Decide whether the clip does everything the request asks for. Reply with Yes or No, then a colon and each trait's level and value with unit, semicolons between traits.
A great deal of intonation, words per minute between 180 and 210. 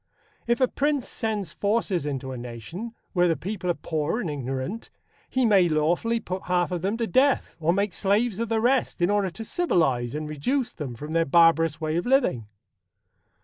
Yes: wide, 6.7 semitones; average, 190 wpm